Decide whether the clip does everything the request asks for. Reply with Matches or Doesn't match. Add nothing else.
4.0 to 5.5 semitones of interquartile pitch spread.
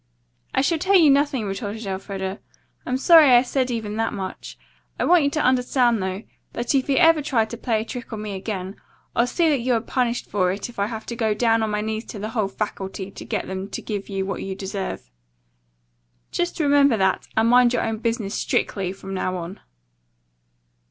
Matches